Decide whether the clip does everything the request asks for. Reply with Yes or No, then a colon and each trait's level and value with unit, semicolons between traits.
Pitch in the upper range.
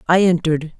No: medium, 170 Hz